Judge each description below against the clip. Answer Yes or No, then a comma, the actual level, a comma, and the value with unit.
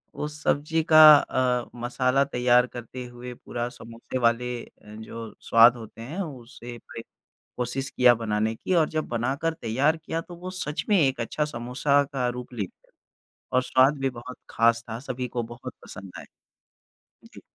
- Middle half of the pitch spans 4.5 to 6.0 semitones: No, average, 2.9 semitones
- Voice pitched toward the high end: No, low, 125 Hz